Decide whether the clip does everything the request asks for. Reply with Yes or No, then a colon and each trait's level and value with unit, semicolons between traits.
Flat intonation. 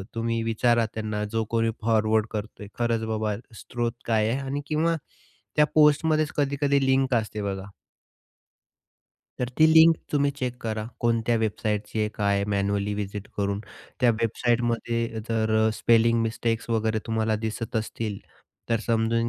Yes: narrow, 1.9 semitones